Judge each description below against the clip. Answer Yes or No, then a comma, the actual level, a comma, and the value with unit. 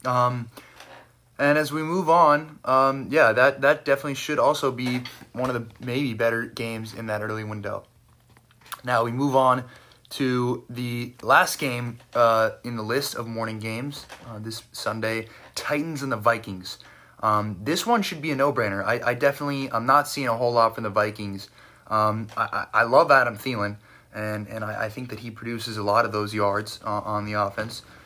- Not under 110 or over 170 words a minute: No, average, 190 wpm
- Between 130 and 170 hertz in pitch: No, low, 120 Hz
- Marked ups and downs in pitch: No, average, 3.7 semitones